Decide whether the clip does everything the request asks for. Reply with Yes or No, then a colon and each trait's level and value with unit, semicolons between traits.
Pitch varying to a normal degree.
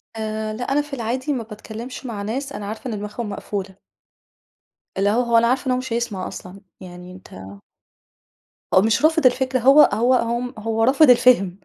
Yes: average, 3.5 semitones